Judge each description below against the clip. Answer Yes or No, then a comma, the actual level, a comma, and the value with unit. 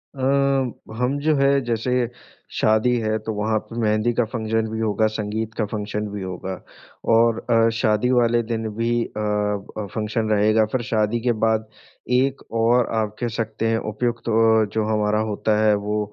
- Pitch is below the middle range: Yes, low, 110 Hz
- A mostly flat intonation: Yes, narrow, 1.5 semitones